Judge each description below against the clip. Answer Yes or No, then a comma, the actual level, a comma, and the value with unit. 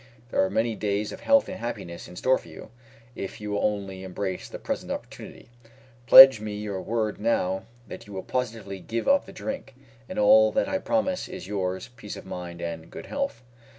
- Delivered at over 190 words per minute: Yes, average, 200 wpm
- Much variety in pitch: Yes, wide, 5.7 semitones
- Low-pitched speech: Yes, low, 105 Hz